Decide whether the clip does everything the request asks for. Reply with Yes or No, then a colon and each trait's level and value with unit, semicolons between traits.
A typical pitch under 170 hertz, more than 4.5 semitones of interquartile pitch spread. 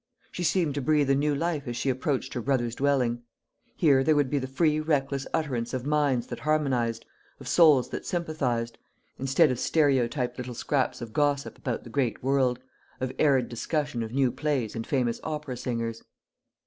No: low, 135 Hz; average, 3.4 semitones